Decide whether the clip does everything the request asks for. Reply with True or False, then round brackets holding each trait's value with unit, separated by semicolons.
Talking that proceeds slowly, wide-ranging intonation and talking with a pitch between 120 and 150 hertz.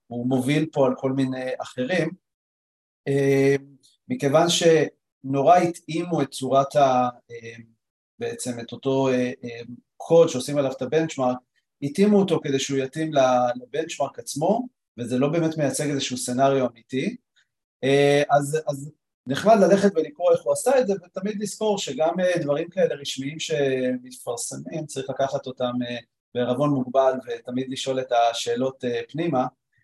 False (125 wpm; 3.8 semitones; 135 Hz)